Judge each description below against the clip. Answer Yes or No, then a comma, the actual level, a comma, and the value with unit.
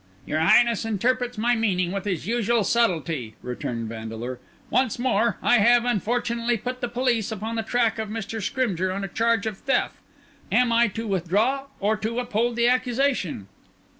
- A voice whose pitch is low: No, high, 225 Hz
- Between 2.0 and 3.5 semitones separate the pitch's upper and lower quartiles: No, average, 3.9 semitones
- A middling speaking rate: Yes, average, 165 wpm